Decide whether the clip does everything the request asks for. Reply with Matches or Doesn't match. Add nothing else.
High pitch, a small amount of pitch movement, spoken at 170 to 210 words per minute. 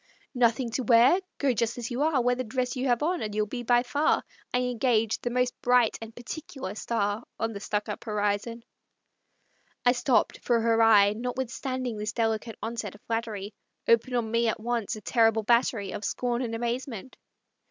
Matches